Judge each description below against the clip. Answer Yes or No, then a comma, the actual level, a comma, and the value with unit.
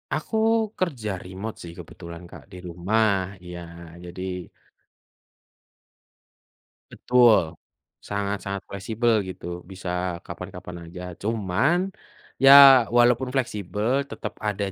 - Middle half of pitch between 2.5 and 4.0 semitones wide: No, average, 4.7 semitones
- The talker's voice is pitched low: Yes, low, 100 Hz